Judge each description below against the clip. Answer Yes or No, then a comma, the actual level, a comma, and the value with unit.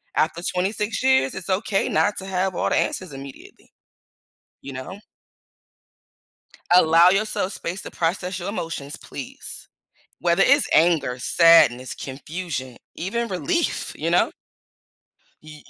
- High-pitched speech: No, medium, 175 Hz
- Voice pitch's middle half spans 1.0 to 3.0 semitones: No, average, 4.2 semitones